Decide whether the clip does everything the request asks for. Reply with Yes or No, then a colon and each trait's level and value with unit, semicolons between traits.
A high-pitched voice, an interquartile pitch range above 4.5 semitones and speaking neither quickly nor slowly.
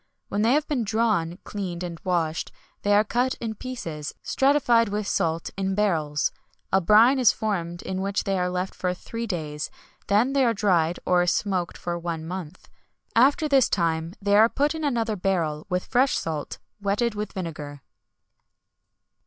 Yes: high, 195 Hz; average, 5.1 semitones; average, 170 wpm